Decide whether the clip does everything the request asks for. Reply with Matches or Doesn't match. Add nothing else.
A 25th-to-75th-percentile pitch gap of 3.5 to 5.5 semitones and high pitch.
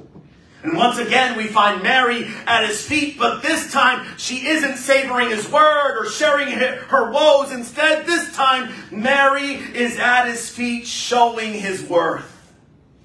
Doesn't match